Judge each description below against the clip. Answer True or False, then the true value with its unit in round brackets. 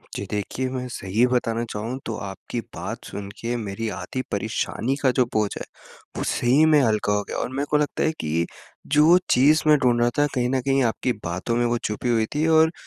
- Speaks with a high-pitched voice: False (120 Hz)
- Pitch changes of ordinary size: True (4.0 semitones)